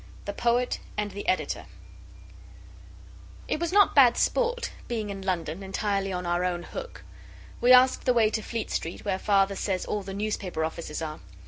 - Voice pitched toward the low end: No, high, 200 Hz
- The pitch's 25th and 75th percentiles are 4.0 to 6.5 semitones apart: Yes, average, 4.5 semitones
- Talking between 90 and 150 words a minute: No, average, 175 wpm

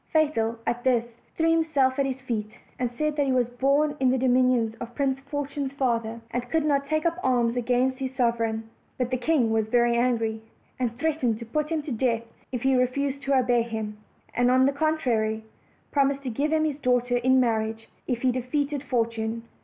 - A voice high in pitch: Yes, very high, 255 Hz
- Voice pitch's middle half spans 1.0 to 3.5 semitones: Yes, average, 3.0 semitones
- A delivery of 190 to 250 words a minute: Yes, average, 200 wpm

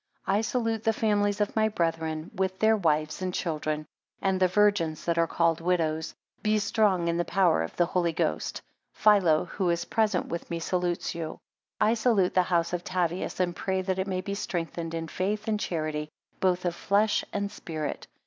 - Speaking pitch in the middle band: Yes, medium, 180 Hz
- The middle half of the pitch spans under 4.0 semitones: Yes, average, 3.4 semitones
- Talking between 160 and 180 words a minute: No, average, 195 wpm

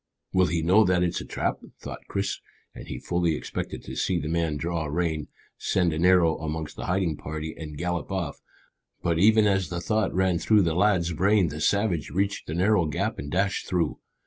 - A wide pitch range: No, average, 3.0 semitones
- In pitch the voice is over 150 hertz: No, very low, 85 Hz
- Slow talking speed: No, fast, 205 wpm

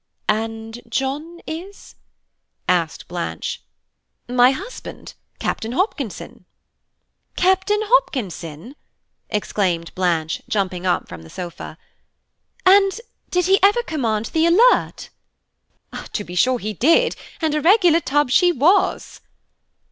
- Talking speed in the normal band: No, slow, 110 wpm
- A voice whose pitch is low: No, very high, 265 Hz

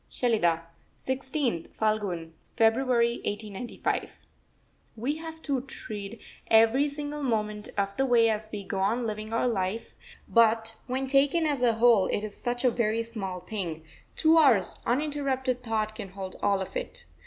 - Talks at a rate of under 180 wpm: Yes, average, 155 wpm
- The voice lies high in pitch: Yes, high, 230 Hz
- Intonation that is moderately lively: Yes, average, 4.0 semitones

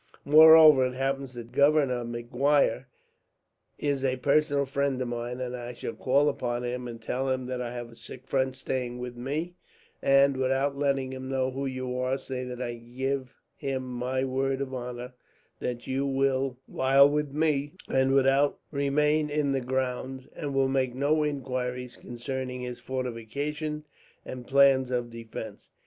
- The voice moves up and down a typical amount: No, narrow, 1.9 semitones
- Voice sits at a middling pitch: No, low, 130 Hz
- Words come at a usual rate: Yes, average, 160 wpm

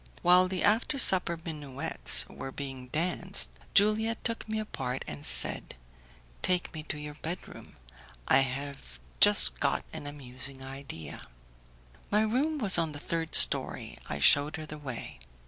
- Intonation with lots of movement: Yes, wide, 5.7 semitones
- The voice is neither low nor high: Yes, medium, 150 Hz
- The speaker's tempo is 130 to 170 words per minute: Yes, average, 145 wpm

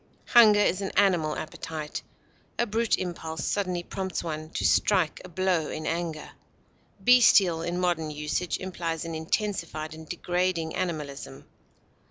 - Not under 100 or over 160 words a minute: Yes, slow, 135 wpm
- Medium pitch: Yes, medium, 170 Hz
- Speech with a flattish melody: No, average, 3.0 semitones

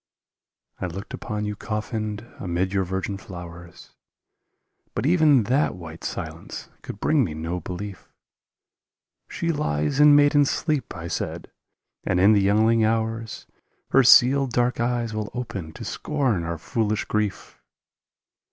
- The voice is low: Yes, low, 105 Hz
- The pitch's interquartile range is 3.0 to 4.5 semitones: No, average, 5.2 semitones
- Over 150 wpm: No, average, 140 wpm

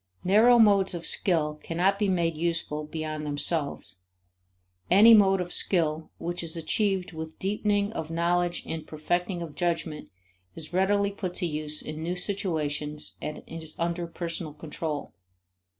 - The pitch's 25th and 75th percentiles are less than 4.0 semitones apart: Yes, average, 3.4 semitones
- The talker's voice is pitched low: No, medium, 170 Hz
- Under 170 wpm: Yes, average, 145 wpm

